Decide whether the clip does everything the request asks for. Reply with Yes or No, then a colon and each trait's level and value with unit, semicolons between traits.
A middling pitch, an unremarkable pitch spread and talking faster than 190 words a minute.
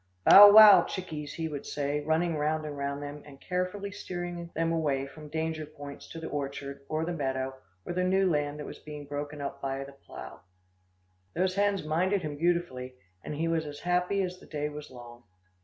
Yes: medium, 155 Hz; average, 3.5 semitones; average, 200 wpm